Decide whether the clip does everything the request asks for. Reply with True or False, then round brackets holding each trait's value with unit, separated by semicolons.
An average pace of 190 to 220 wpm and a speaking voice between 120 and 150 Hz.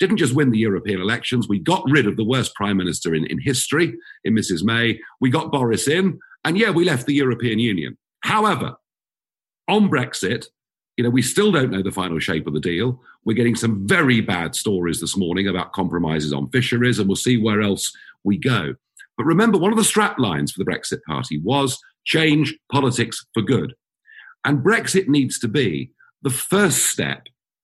True (195 wpm; 125 Hz)